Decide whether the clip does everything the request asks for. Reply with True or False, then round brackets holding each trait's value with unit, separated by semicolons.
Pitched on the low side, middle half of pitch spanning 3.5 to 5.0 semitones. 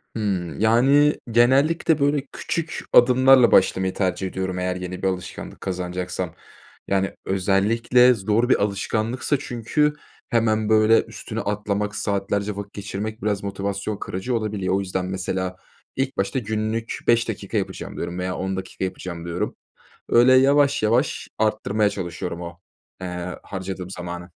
True (100 Hz; 3.9 semitones)